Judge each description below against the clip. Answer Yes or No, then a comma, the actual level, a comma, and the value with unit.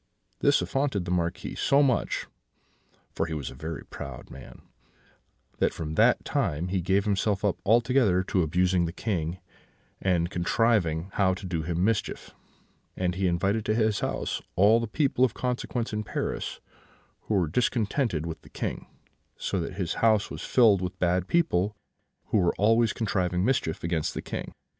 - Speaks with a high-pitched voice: No, very low, 95 Hz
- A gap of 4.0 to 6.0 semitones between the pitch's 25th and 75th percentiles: Yes, average, 4.5 semitones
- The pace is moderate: Yes, average, 165 wpm